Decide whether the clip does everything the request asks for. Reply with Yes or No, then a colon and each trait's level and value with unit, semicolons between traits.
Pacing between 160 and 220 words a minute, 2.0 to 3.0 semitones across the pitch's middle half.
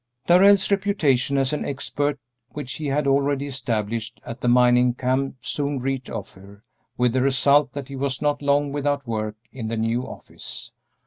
Yes: average, 170 wpm; average, 2.7 semitones